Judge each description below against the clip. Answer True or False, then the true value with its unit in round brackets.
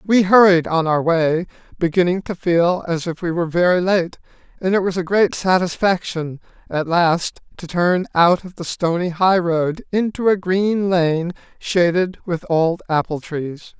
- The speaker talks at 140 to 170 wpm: True (165 wpm)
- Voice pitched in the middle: True (175 Hz)